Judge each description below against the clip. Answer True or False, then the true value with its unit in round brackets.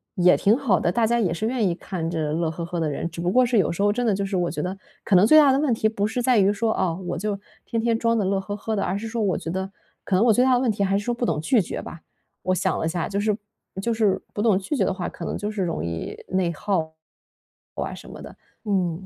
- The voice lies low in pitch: False (200 Hz)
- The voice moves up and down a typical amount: True (4.1 semitones)